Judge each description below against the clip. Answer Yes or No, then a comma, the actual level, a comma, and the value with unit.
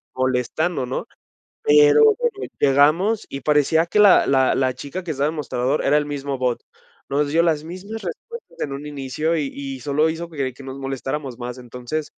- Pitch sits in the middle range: Yes, medium, 145 Hz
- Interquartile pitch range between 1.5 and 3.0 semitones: No, average, 4.0 semitones